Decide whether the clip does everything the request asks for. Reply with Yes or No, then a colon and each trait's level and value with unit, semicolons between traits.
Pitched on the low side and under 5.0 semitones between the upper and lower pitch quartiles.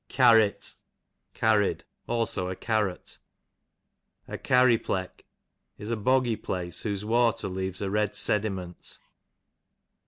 Yes: low, 105 Hz; average, 3.3 semitones